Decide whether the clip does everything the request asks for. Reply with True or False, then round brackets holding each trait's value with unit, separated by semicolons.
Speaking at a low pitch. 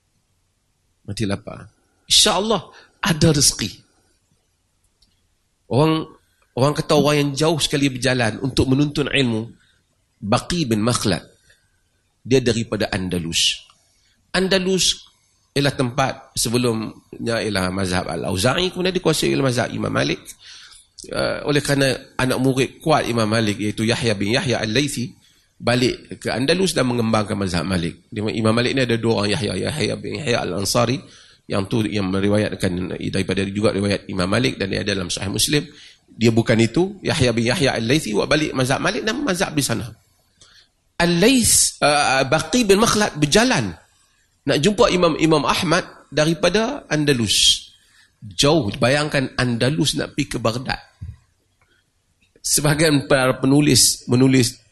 True (120 Hz)